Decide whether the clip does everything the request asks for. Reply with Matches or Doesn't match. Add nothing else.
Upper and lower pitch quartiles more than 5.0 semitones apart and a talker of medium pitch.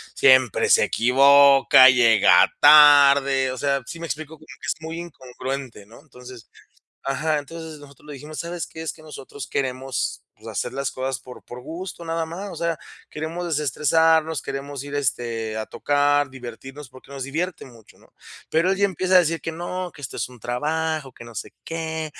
Doesn't match